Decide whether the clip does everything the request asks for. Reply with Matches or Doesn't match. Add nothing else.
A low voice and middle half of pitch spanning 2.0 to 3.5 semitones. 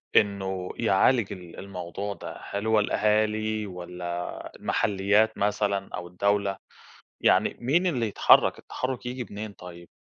Matches